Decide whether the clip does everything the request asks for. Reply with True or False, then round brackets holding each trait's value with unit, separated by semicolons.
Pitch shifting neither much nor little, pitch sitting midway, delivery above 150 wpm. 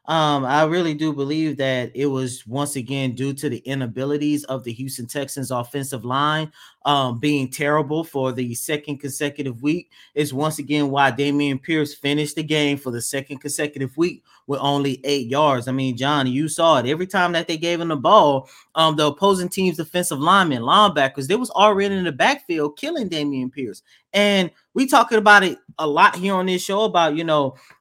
True (3.3 semitones; 145 Hz; 195 wpm)